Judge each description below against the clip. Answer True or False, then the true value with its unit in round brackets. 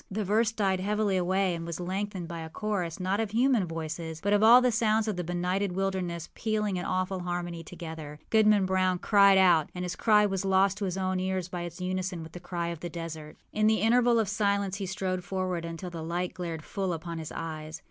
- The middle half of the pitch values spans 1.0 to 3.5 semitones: True (2.9 semitones)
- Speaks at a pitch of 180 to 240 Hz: True (185 Hz)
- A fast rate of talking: True (225 wpm)